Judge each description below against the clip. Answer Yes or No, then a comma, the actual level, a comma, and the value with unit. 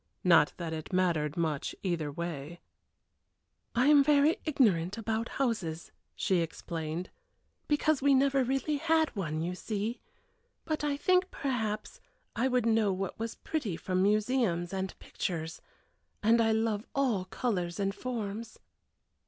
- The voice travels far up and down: Yes, wide, 7.1 semitones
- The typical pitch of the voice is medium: No, high, 215 Hz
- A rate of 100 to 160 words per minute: Yes, slow, 135 wpm